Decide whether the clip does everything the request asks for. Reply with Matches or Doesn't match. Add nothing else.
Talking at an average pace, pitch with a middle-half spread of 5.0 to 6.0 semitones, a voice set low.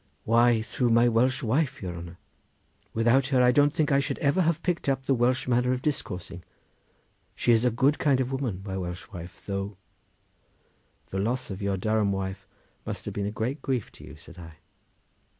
Matches